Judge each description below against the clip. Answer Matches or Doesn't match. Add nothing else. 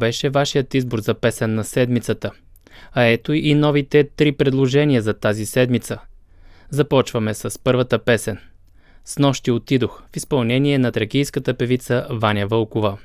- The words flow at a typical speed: Matches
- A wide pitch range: Doesn't match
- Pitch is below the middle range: Matches